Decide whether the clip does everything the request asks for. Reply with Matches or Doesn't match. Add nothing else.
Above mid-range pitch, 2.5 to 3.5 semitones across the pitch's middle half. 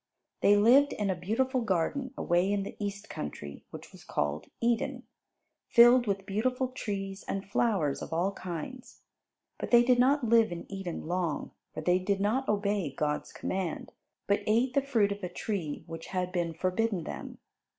Doesn't match